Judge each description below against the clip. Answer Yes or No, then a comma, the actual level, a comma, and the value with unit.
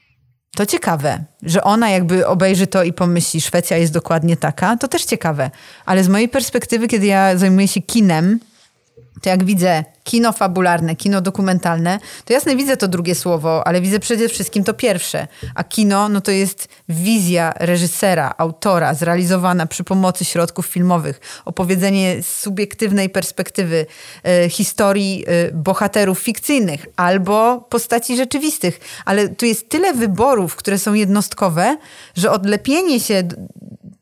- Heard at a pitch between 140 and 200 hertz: Yes, high, 190 Hz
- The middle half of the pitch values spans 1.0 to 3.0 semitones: No, average, 3.4 semitones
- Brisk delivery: No, average, 140 wpm